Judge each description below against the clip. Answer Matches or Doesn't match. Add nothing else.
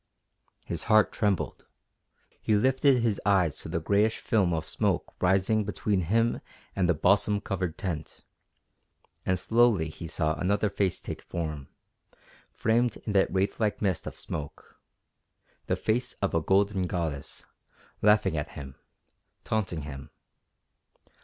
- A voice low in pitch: Matches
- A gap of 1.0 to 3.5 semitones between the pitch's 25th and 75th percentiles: Doesn't match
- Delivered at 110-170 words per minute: Matches